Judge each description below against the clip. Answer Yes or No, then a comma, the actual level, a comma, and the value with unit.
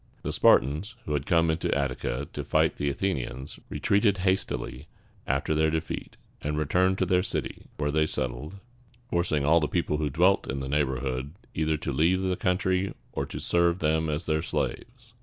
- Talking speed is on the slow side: No, average, 175 wpm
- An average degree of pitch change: Yes, average, 4.0 semitones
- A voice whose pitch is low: Yes, very low, 80 Hz